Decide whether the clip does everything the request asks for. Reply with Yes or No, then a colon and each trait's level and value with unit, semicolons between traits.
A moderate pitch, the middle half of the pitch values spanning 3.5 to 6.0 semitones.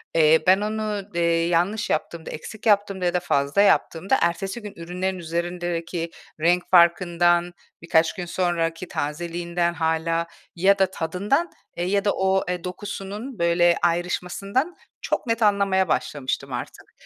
No: medium, 175 Hz; average, 2.7 semitones